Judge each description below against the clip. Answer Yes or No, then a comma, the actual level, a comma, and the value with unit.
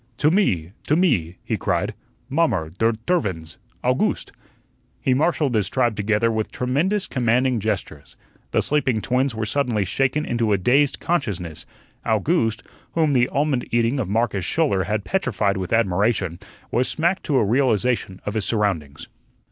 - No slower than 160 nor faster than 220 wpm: No, average, 150 wpm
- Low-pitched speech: Yes, low, 115 Hz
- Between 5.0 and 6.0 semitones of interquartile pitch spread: Yes, wide, 5.5 semitones